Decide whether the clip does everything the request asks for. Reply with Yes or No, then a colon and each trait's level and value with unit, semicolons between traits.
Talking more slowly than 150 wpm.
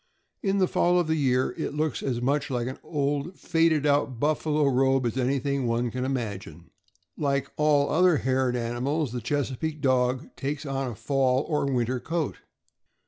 No: average, 175 wpm